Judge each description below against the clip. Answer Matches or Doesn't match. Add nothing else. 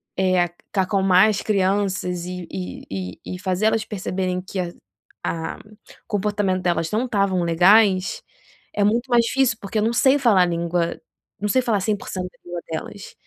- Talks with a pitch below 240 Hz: Matches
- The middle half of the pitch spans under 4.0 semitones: Matches